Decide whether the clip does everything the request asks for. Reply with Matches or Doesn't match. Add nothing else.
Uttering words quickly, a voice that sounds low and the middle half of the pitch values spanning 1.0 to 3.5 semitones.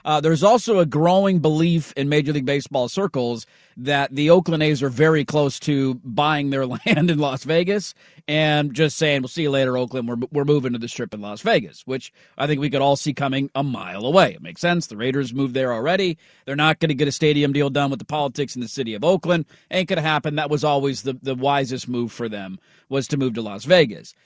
Doesn't match